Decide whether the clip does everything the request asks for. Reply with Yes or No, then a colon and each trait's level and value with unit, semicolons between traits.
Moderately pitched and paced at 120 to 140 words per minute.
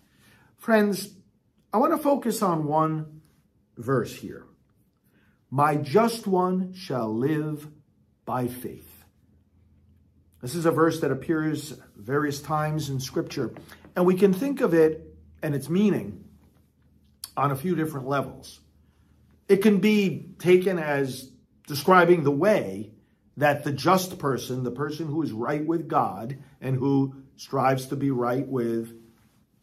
Yes: medium, 145 Hz; slow, 135 wpm